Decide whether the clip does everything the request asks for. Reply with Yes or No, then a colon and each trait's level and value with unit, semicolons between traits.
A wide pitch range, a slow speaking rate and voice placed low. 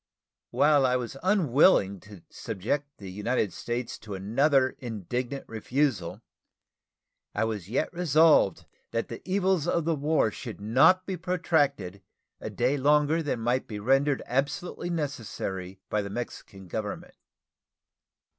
Yes: wide, 6.0 semitones; slow, 130 wpm; low, 130 Hz